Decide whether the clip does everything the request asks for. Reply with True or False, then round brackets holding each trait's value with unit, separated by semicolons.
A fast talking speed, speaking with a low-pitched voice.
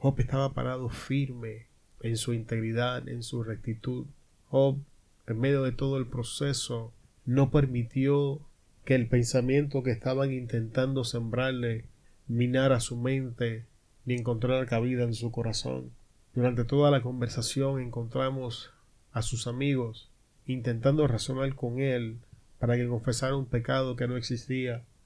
False (130 wpm; 125 Hz)